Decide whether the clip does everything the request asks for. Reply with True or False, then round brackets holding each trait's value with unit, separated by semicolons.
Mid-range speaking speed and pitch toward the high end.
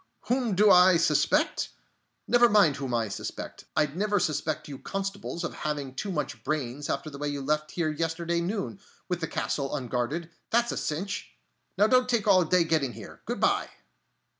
False (180 wpm; 165 Hz)